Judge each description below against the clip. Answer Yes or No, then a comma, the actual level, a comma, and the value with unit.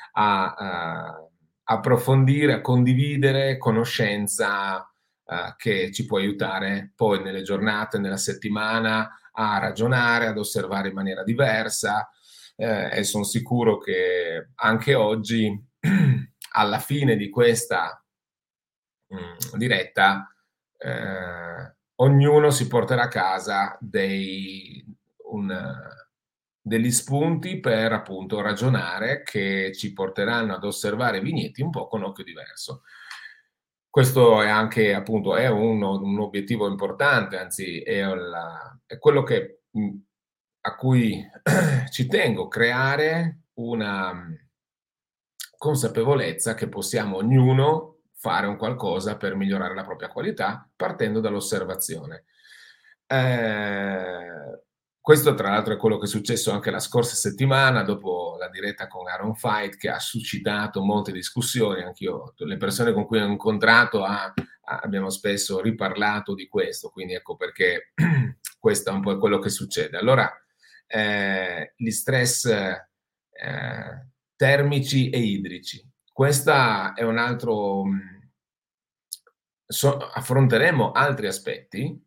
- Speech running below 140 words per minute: Yes, slow, 115 wpm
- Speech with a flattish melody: No, average, 5.1 semitones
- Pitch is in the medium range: No, low, 115 Hz